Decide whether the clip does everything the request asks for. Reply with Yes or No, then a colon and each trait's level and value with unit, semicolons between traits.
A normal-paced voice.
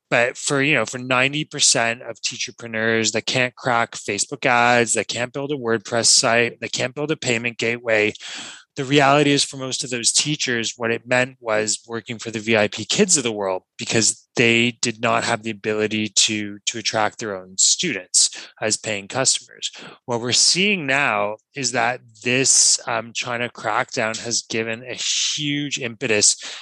Yes: average, 170 wpm